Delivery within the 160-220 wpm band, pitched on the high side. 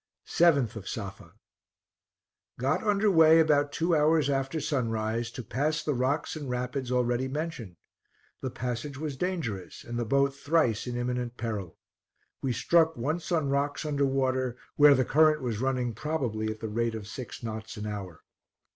No: average, 165 wpm; low, 130 Hz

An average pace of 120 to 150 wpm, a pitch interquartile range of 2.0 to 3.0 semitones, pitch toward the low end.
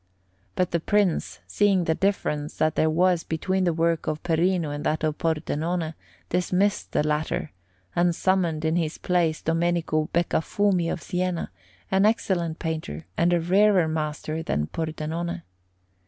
No: average, 145 wpm; narrow, 2.4 semitones; medium, 165 Hz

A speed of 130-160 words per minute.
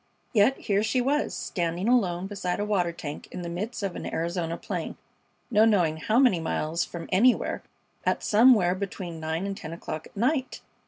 No: average, 180 wpm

